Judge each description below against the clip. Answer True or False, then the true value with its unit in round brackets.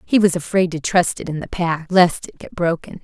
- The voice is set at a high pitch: False (175 Hz)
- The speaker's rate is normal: False (255 wpm)